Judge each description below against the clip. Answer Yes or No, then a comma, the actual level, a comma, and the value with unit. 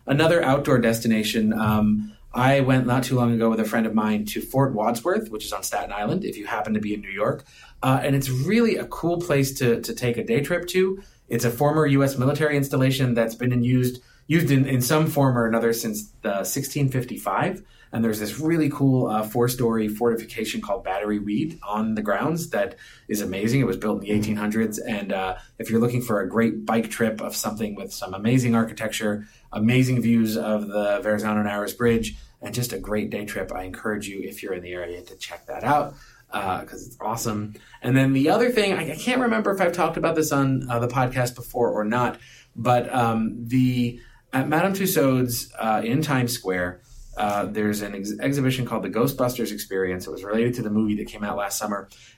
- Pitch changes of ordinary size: Yes, average, 3.9 semitones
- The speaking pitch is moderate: No, low, 120 Hz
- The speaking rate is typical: No, fast, 215 wpm